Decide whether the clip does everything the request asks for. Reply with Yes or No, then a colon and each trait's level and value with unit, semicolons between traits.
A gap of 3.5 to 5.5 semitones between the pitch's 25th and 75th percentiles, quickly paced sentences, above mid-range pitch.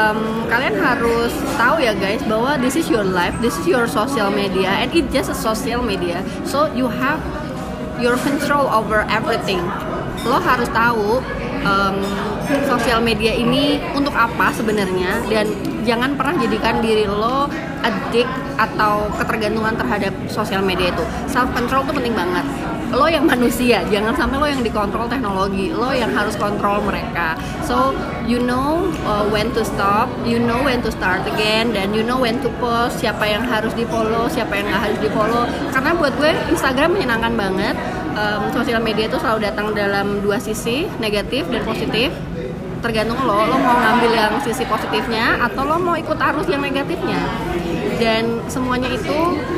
No: average, 2.9 semitones; fast, 165 wpm; high, 230 Hz